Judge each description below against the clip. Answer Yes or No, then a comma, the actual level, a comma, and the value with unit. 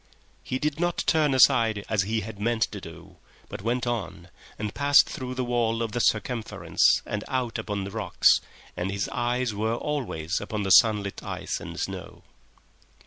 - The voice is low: Yes, low, 115 Hz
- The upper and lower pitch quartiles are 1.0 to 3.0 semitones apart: No, average, 3.4 semitones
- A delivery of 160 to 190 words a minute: Yes, average, 175 wpm